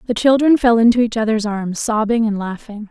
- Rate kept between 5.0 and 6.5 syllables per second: Yes, 5.5 syllables/s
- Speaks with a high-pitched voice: Yes, high, 225 Hz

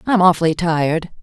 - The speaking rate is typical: Yes, average, 145 wpm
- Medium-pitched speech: Yes, medium, 170 Hz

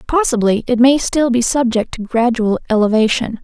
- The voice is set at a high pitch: Yes, high, 240 Hz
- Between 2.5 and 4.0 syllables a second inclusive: No, 5.1 syllables/s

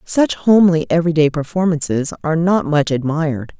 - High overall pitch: No, medium, 160 Hz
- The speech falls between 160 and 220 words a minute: No, slow, 135 wpm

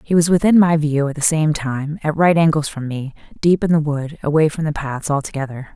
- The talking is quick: Yes, fast, 240 wpm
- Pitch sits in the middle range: Yes, medium, 150 Hz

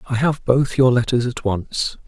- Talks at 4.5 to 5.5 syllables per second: No, 4.2 syllables/s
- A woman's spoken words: No, male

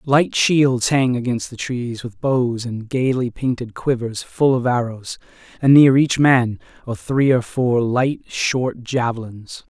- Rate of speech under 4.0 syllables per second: Yes, 3.8 syllables/s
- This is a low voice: Yes, low, 125 Hz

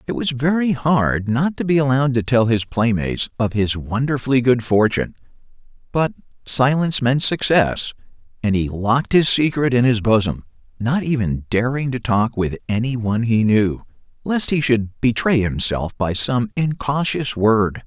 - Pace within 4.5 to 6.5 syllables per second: Yes, 4.7 syllables/s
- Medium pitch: No, low, 120 Hz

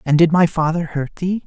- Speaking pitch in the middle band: Yes, medium, 165 Hz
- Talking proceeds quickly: Yes, fast, 245 wpm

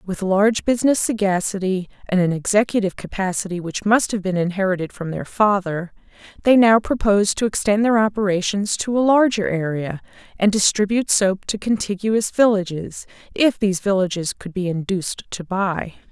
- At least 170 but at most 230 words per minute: No, average, 155 wpm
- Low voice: No, high, 200 Hz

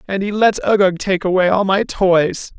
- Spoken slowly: No, fast, 210 wpm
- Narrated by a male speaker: Yes, male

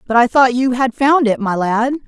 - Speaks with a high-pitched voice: Yes, high, 245 Hz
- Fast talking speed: Yes, fast, 260 wpm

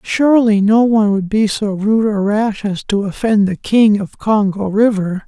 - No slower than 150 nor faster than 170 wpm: No, average, 195 wpm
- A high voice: Yes, high, 210 Hz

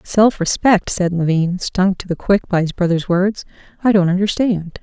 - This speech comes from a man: No, female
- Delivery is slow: No, average, 185 wpm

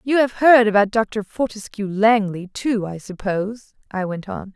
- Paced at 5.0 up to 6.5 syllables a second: No, 4.5 syllables/s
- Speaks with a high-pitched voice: Yes, high, 210 Hz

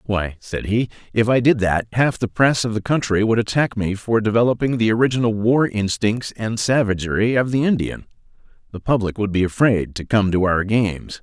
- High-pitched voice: No, low, 110 Hz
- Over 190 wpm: Yes, average, 200 wpm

